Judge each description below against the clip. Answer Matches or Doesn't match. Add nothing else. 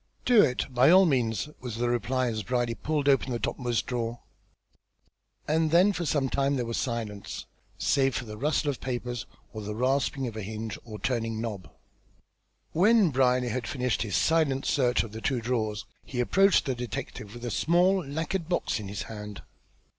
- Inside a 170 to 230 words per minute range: Matches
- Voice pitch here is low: Matches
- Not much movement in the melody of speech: Doesn't match